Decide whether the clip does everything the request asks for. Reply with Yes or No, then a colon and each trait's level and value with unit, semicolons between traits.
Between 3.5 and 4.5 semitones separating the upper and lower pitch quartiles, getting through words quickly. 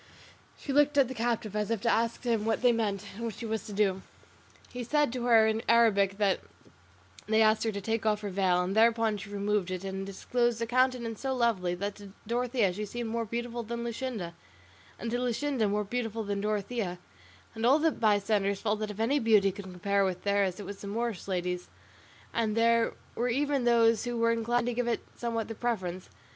No: average, 2.9 semitones; fast, 210 wpm